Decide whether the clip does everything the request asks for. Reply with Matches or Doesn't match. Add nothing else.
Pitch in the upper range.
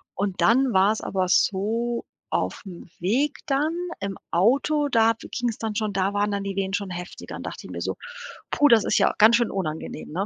Matches